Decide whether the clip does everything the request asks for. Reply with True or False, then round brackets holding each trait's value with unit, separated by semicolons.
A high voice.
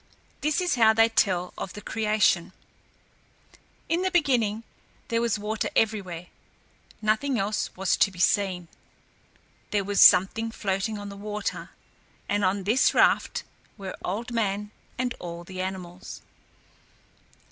True (205 Hz)